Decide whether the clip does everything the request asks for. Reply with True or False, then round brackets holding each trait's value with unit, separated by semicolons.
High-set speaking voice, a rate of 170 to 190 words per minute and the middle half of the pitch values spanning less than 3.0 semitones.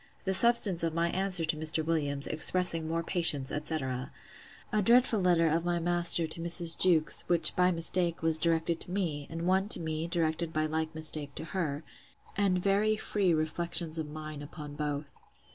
False (165 Hz; 180 wpm; 2.4 semitones)